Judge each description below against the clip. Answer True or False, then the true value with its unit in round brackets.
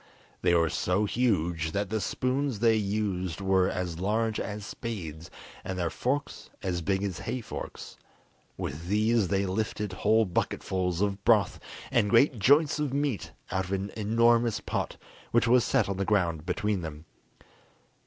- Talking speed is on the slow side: False (160 wpm)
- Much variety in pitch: False (3.7 semitones)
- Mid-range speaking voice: False (100 Hz)